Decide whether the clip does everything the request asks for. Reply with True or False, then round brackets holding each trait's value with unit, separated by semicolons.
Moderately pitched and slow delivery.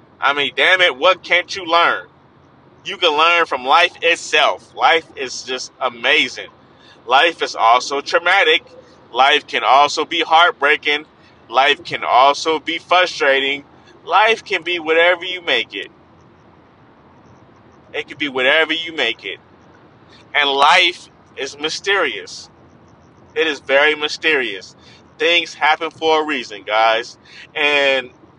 True (160 Hz; 130 wpm)